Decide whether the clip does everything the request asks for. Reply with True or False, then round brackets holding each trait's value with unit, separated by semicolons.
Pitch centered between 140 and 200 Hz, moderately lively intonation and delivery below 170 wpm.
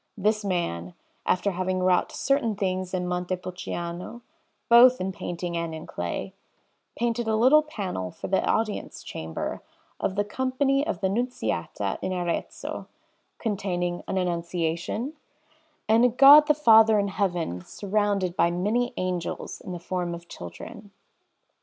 True (185 Hz; 4.2 semitones; 140 wpm)